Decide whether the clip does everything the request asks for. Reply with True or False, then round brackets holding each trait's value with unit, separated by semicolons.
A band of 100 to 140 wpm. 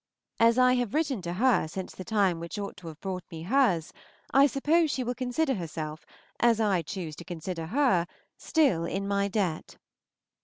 False (185 wpm)